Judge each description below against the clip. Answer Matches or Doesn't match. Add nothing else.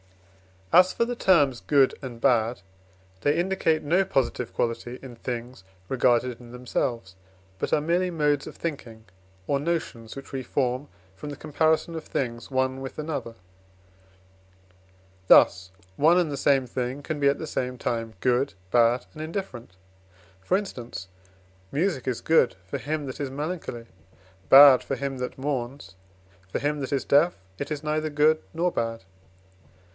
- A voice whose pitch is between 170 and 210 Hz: Doesn't match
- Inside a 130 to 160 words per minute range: Matches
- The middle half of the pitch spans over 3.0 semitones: Matches